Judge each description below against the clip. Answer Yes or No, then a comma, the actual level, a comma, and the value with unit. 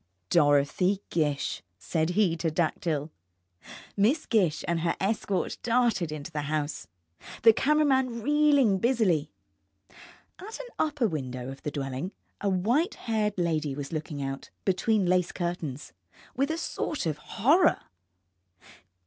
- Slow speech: Yes, slow, 130 wpm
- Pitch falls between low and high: Yes, medium, 180 Hz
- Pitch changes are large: Yes, wide, 7.5 semitones